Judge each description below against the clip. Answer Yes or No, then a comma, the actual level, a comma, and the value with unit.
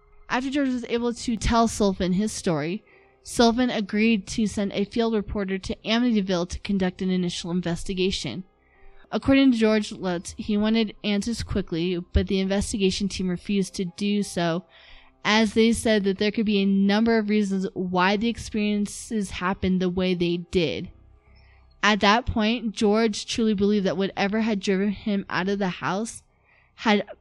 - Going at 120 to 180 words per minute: Yes, average, 165 wpm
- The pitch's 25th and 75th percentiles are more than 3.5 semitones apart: No, average, 2.8 semitones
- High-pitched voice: Yes, high, 200 Hz